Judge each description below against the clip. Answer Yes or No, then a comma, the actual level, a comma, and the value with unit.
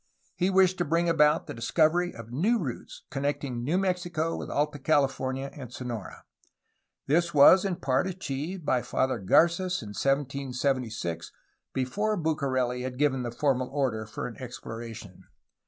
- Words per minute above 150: No, average, 145 wpm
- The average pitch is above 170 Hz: No, medium, 140 Hz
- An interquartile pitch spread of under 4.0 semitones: No, average, 5.0 semitones